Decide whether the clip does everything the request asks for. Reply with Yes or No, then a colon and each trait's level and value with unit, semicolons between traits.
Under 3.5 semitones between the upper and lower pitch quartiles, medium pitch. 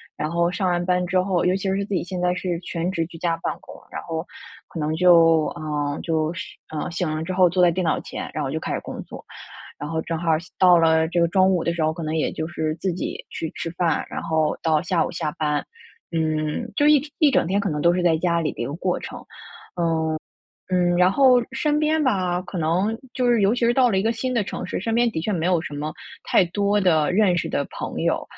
Yes: average, 2.8 semitones; medium, 175 Hz